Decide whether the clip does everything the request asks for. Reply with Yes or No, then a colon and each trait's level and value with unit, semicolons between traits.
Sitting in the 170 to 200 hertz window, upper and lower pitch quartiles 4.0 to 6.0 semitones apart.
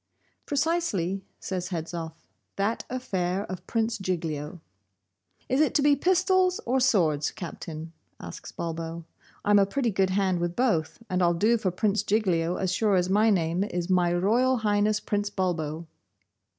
Yes: high, 190 Hz; average, 4.5 semitones